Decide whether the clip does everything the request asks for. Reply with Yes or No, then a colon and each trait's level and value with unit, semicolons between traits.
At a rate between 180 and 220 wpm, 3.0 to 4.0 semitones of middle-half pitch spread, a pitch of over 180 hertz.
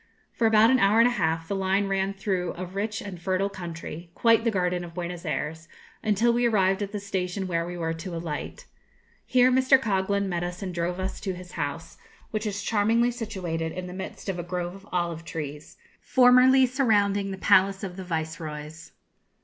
Yes: average, 200 wpm; average, 3.4 semitones; high, 190 Hz